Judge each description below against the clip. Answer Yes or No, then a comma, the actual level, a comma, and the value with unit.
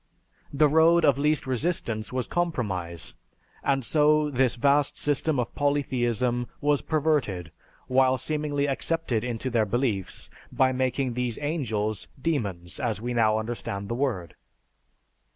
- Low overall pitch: Yes, low, 130 Hz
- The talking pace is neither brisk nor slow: No, slow, 130 wpm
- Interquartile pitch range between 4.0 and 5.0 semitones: Yes, average, 4.5 semitones